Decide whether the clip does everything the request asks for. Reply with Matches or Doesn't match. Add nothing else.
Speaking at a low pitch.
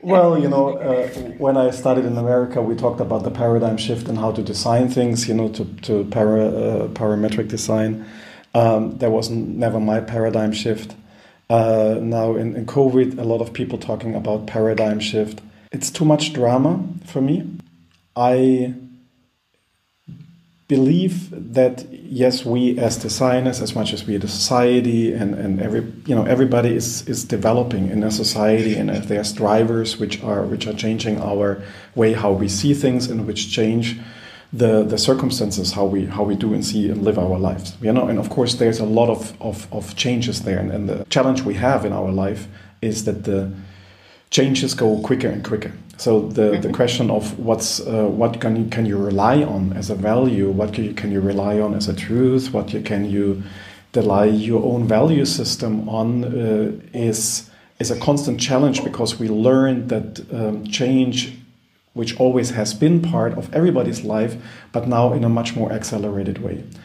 Matches